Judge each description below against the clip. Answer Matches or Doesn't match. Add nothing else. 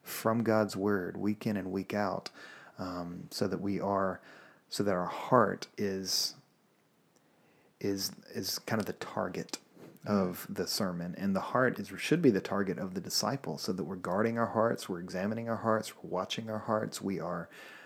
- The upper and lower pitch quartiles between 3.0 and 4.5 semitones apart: Doesn't match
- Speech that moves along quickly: Doesn't match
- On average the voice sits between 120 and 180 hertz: Doesn't match